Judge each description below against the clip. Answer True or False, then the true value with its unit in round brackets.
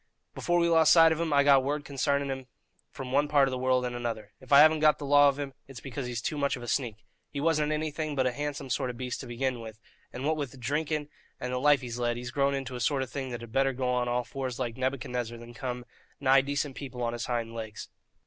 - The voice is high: False (135 Hz)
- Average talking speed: False (265 wpm)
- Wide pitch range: False (2.8 semitones)